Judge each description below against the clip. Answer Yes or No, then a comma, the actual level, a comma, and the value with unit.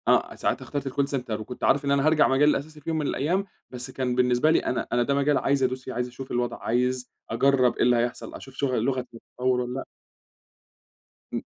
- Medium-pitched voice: No, low, 130 Hz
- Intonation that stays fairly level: Yes, narrow, 2.2 semitones